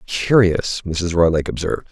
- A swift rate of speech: No, slow, 125 wpm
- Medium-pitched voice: No, very low, 90 Hz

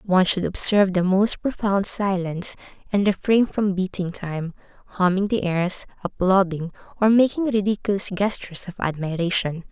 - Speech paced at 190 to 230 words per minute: No, slow, 135 wpm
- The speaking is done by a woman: Yes, female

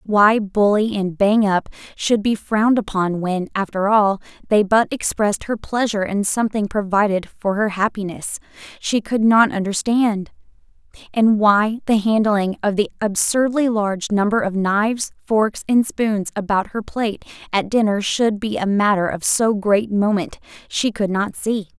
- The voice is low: No, high, 210 Hz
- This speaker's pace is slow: No, average, 160 wpm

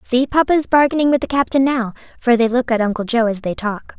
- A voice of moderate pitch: No, high, 245 Hz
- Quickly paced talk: Yes, fast, 255 wpm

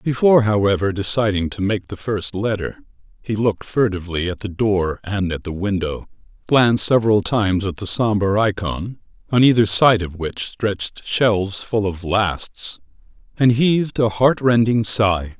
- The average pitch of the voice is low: Yes, low, 105 Hz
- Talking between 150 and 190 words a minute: Yes, average, 160 wpm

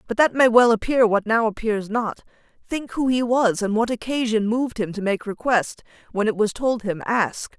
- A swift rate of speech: Yes, fast, 215 wpm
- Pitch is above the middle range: Yes, high, 225 Hz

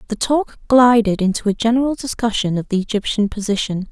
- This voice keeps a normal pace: Yes, average, 170 wpm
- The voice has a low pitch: No, high, 220 Hz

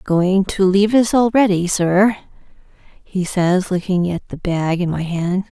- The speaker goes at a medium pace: Yes, average, 160 wpm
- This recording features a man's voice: No, female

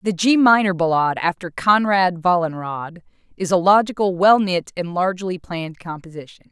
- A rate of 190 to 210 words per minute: No, average, 145 wpm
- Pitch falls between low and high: Yes, medium, 180 Hz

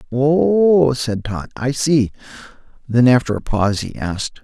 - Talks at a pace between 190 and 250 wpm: No, average, 150 wpm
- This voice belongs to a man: Yes, male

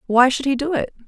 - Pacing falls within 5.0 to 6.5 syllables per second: Yes, 6.1 syllables/s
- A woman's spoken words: Yes, female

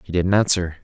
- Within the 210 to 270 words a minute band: Yes, fast, 215 wpm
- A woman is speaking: No, male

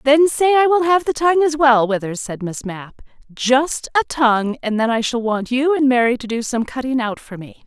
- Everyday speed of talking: No, fast, 235 wpm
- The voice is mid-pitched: No, very high, 255 Hz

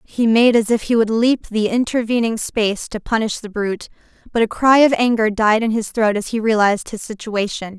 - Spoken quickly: Yes, fast, 215 wpm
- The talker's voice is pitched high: Yes, high, 220 Hz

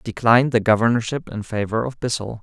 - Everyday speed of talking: Yes, average, 175 wpm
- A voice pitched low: Yes, low, 115 Hz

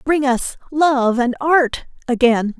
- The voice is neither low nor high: No, very high, 265 Hz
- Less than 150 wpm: Yes, average, 140 wpm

